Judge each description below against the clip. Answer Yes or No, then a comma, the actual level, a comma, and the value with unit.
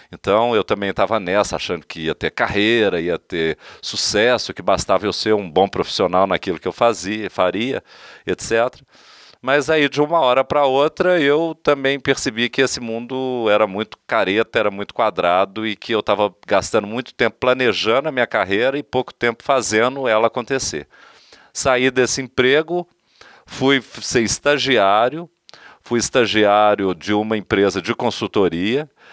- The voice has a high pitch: No, low, 120 Hz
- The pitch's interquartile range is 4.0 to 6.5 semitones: Yes, average, 4.6 semitones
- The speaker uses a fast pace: No, average, 155 wpm